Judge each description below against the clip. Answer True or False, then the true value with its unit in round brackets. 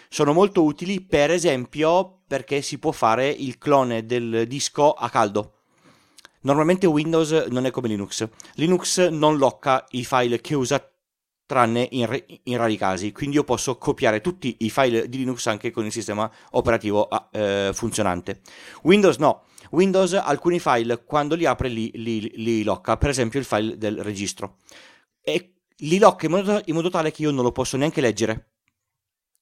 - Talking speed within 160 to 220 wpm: True (170 wpm)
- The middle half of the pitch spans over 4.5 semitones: True (5.2 semitones)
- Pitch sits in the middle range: False (130 Hz)